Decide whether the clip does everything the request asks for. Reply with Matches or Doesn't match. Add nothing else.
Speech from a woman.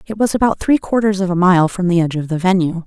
Matches